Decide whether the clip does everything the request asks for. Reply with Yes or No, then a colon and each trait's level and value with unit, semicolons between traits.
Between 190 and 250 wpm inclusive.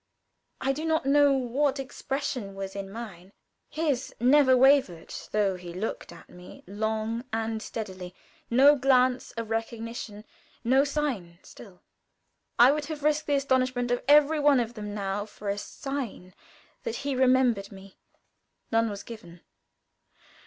No: average, 145 wpm